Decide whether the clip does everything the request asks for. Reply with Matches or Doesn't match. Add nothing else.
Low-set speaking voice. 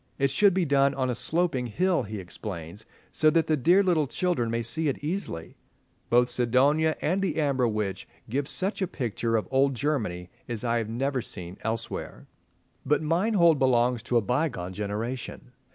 Matches